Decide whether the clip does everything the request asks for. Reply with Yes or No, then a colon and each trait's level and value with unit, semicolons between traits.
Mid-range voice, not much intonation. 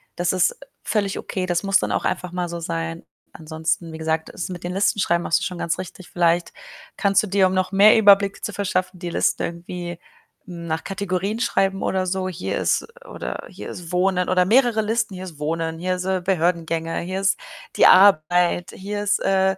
Yes: medium, 180 Hz; narrow, 2.3 semitones